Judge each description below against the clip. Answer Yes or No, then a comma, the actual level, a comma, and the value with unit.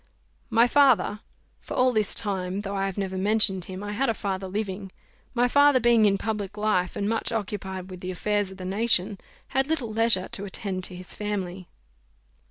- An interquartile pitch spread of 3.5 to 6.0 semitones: No, average, 2.9 semitones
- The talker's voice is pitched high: Yes, high, 205 Hz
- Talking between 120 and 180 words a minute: No, average, 190 wpm